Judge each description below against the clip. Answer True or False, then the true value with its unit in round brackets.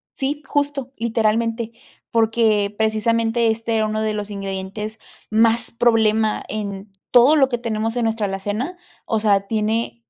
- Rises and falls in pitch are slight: True (1.7 semitones)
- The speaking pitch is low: False (220 Hz)